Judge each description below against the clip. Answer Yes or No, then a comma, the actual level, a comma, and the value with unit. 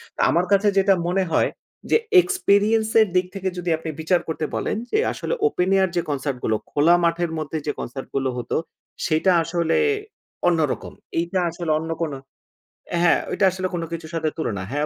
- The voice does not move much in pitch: No, average, 3.2 semitones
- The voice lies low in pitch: No, medium, 170 Hz